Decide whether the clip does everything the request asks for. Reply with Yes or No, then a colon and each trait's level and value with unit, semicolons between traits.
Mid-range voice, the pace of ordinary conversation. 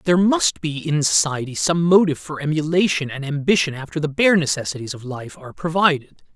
Yes: medium, 155 Hz; average, 180 wpm